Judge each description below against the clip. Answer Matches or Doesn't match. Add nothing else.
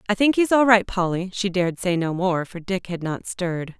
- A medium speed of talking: Doesn't match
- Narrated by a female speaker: Matches